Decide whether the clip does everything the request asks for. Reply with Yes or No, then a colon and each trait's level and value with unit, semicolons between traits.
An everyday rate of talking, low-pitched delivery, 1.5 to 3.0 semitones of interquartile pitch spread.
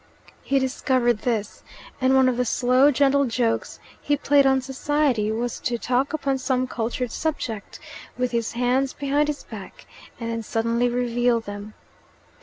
No: average, 155 wpm; very high, 250 Hz; average, 2.7 semitones